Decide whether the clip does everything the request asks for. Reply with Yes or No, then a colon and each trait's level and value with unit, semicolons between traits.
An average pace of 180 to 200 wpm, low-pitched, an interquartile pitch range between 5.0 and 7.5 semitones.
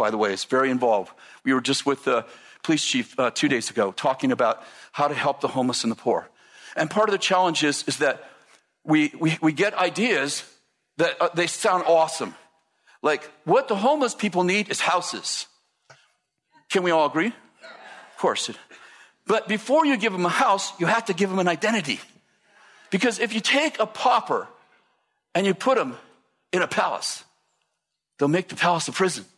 No: average, 190 wpm; medium, 185 Hz; wide, 5.6 semitones